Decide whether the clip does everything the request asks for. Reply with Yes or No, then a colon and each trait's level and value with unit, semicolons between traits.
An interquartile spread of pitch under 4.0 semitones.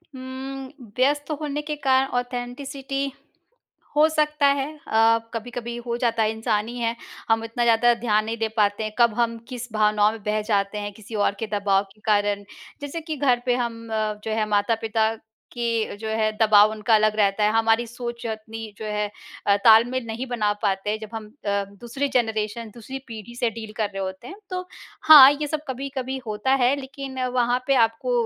Yes: average, 3.3 semitones